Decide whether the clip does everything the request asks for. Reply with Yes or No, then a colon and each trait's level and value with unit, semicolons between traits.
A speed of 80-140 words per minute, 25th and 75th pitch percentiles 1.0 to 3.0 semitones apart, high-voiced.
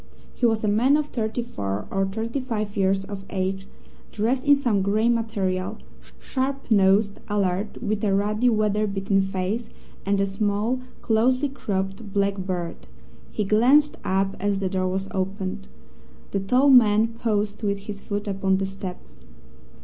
No: average, 155 wpm; average, 2.7 semitones; high, 205 Hz